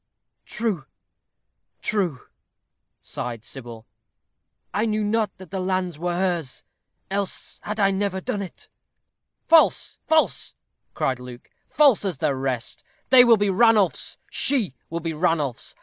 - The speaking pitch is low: No, medium, 185 Hz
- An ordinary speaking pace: No, slow, 130 wpm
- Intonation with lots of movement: Yes, wide, 6.4 semitones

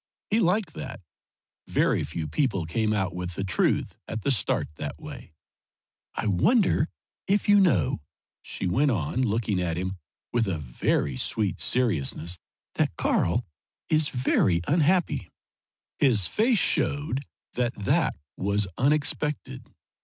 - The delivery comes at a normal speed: No, slow, 130 wpm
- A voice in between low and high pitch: No, low, 115 Hz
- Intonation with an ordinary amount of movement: No, wide, 8.5 semitones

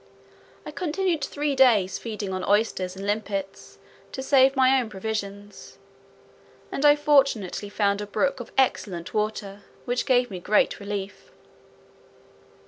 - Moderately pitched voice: No, high, 215 Hz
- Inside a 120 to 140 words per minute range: Yes, slow, 135 wpm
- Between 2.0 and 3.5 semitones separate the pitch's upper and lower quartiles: No, average, 4.9 semitones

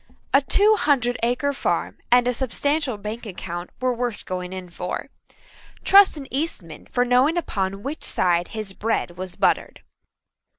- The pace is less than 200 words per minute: Yes, average, 155 wpm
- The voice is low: No, high, 240 Hz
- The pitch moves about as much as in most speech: No, wide, 6.6 semitones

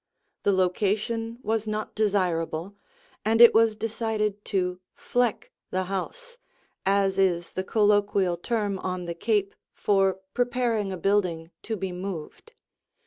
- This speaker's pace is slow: Yes, slow, 130 wpm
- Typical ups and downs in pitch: Yes, average, 3.0 semitones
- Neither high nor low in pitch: No, high, 200 Hz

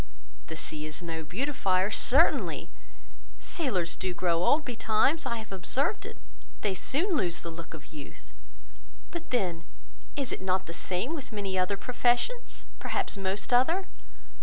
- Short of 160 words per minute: Yes, average, 150 wpm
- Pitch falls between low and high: No, high, 195 Hz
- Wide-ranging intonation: Yes, wide, 7.1 semitones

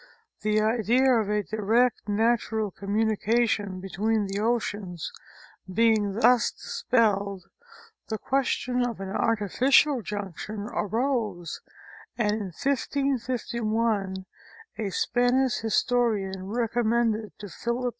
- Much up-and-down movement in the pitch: No, average, 2.9 semitones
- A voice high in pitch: Yes, high, 220 Hz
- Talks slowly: Yes, slow, 100 wpm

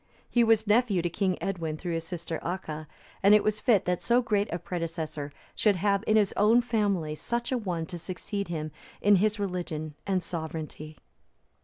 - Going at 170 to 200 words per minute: Yes, average, 185 wpm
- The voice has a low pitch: No, medium, 185 Hz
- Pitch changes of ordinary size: Yes, average, 4.3 semitones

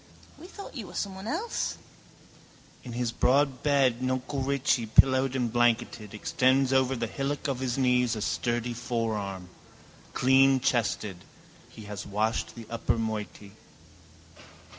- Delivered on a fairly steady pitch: No, average, 3.0 semitones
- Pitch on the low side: Yes, low, 125 Hz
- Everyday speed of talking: No, slow, 130 wpm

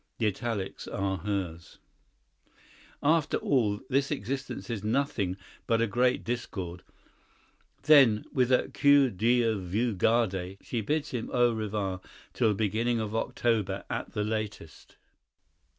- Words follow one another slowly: Yes, slow, 130 wpm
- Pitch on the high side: No, low, 110 Hz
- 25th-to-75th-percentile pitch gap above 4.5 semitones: No, average, 3.7 semitones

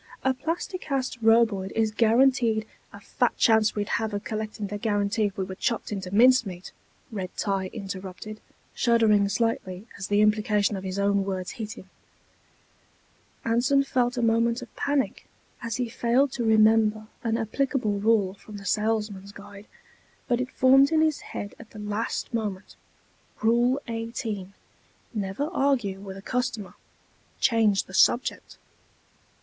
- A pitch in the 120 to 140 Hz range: No, high, 220 Hz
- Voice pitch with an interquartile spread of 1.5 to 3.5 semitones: Yes, average, 2.9 semitones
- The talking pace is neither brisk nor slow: Yes, average, 150 wpm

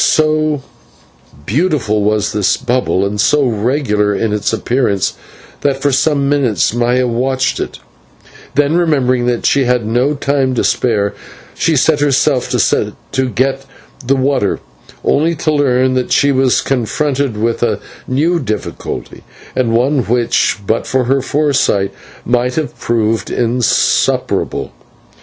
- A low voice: Yes, low, 130 Hz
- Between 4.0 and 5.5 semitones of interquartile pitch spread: No, average, 3.5 semitones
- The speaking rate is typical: No, slow, 130 wpm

